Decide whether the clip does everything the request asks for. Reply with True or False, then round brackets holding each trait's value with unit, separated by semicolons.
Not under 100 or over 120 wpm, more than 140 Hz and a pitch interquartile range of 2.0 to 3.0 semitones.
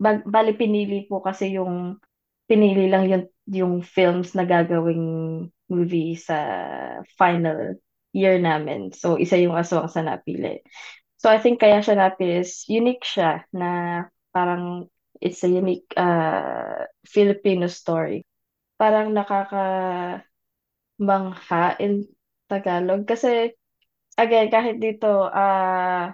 True (115 wpm; 185 Hz; 2.7 semitones)